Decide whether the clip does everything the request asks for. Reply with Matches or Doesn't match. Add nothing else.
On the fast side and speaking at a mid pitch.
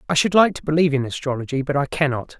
Matches